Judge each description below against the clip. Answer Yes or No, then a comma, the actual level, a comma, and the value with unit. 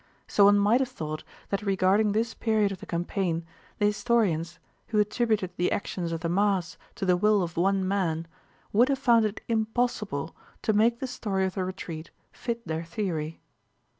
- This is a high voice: Yes, high, 200 Hz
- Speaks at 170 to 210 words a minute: Yes, average, 180 wpm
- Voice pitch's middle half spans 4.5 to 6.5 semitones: No, average, 3.9 semitones